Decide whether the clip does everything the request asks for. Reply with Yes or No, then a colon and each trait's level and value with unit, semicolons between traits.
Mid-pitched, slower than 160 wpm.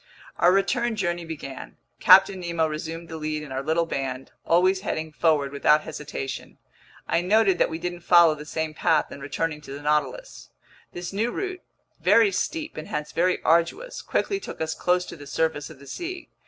No: medium, 165 Hz; average, 185 wpm